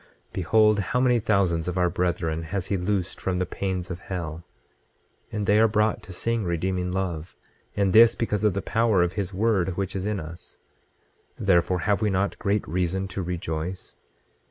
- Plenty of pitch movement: No, average, 2.8 semitones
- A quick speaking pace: No, average, 185 wpm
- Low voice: Yes, very low, 95 Hz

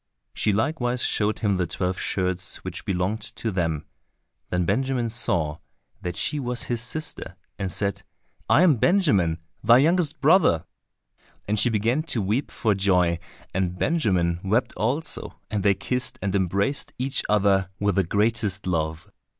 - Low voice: Yes, low, 100 Hz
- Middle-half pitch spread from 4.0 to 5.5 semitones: Yes, average, 4.9 semitones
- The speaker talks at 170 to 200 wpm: No, average, 150 wpm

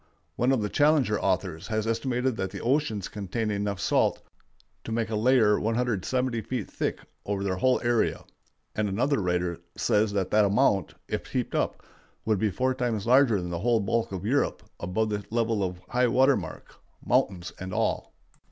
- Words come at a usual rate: Yes, average, 180 wpm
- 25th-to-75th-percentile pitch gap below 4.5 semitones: Yes, average, 3.9 semitones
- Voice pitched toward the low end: Yes, low, 110 Hz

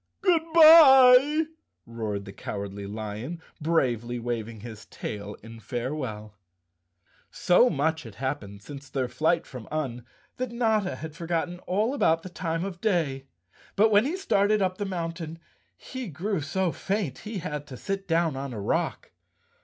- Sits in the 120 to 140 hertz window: No, medium, 160 Hz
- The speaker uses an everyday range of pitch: No, wide, 8.8 semitones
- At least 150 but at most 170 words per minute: Yes, average, 155 wpm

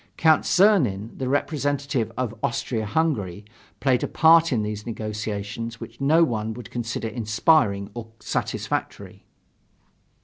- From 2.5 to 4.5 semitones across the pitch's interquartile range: No, average, 5.0 semitones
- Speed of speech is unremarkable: No, slow, 125 wpm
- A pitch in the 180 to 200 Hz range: No, low, 115 Hz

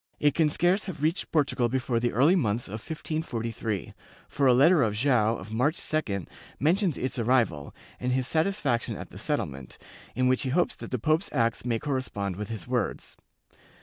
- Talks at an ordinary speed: Yes, average, 180 wpm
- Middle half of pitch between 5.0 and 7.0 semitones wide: Yes, wide, 5.4 semitones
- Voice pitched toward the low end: Yes, low, 130 Hz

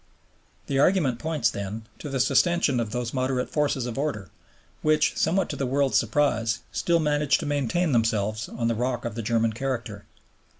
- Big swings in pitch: No, average, 4.3 semitones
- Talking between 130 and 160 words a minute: No, average, 175 wpm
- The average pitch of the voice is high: No, low, 130 Hz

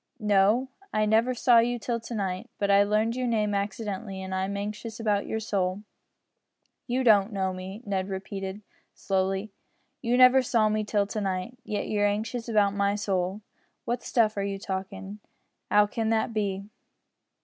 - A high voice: Yes, high, 210 Hz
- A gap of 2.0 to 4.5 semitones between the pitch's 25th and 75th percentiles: Yes, narrow, 2.5 semitones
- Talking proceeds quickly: No, average, 170 wpm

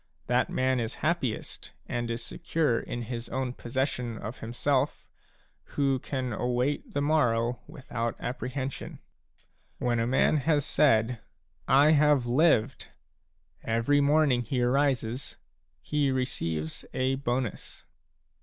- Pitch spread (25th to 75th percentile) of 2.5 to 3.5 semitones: Yes, average, 2.9 semitones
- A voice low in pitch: Yes, low, 130 Hz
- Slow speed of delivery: Yes, slow, 120 wpm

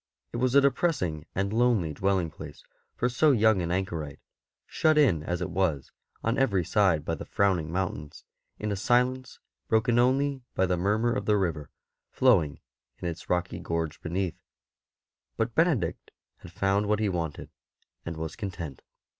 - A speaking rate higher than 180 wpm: No, average, 165 wpm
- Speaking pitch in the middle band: No, very low, 95 Hz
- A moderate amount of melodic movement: No, wide, 6.1 semitones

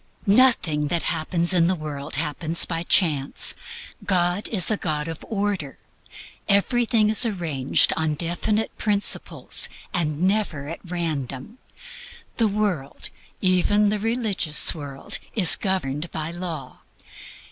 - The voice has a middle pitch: Yes, medium, 175 Hz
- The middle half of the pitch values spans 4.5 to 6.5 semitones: Yes, average, 5.1 semitones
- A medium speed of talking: No, slow, 120 wpm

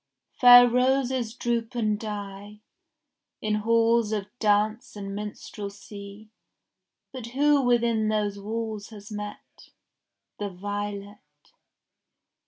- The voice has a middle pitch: No, high, 215 Hz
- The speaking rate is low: Yes, slow, 95 wpm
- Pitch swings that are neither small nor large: No, narrow, 2.3 semitones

